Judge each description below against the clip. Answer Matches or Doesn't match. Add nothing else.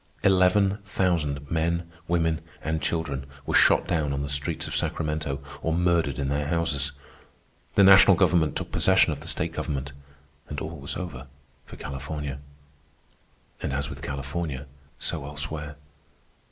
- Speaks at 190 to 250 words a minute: Doesn't match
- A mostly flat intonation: Doesn't match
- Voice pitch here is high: Doesn't match